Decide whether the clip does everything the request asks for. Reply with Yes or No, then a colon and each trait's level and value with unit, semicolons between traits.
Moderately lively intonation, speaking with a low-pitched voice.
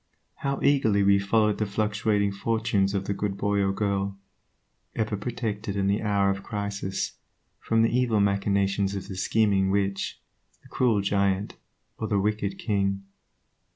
No: narrow, 1.6 semitones; low, 100 Hz